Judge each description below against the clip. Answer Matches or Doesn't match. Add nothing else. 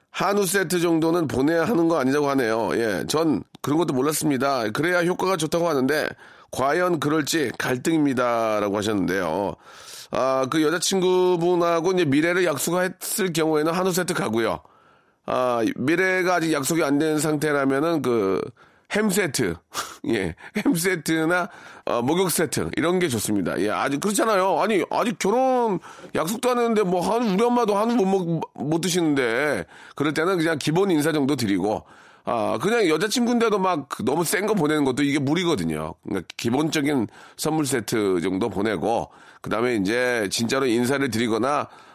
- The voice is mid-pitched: Matches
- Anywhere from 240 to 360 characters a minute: Matches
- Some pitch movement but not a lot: Matches